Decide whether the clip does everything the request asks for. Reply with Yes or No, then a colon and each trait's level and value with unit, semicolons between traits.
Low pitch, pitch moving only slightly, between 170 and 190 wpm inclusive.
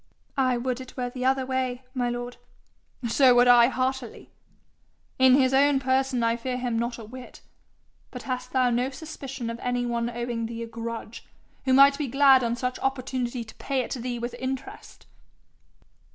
No: very high, 250 Hz; narrow, 1.7 semitones; average, 180 wpm